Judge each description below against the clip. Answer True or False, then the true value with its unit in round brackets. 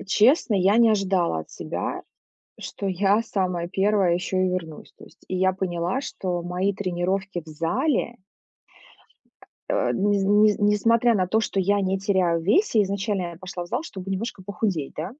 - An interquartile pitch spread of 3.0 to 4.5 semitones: False (2.4 semitones)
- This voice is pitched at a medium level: False (195 Hz)